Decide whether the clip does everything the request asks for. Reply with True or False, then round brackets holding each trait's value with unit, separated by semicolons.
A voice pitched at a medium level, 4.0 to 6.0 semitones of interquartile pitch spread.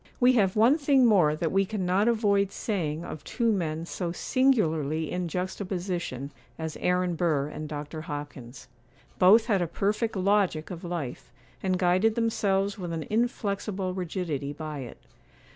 True (180 Hz; 4.6 semitones)